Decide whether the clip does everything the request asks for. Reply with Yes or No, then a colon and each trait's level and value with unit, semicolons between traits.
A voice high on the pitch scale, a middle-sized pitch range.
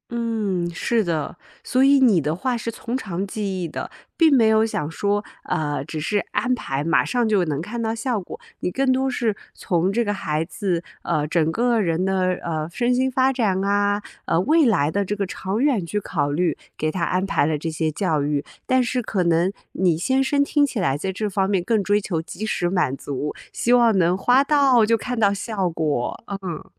No: high, 195 Hz; wide, 5.8 semitones